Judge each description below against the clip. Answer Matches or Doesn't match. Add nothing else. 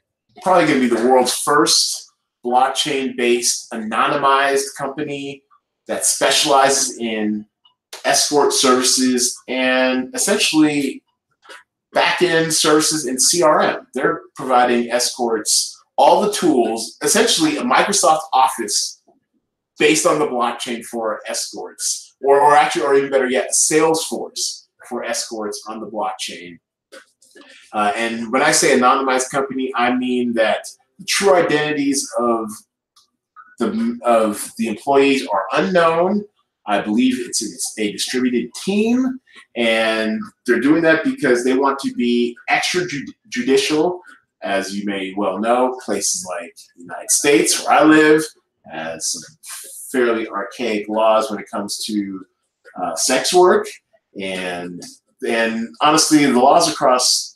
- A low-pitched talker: Matches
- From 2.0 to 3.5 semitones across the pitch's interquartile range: Doesn't match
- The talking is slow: Matches